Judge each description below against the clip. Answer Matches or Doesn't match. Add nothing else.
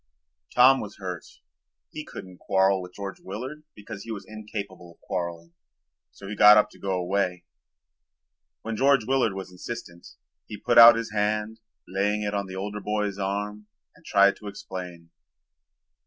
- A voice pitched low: Matches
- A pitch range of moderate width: Doesn't match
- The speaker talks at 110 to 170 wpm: Matches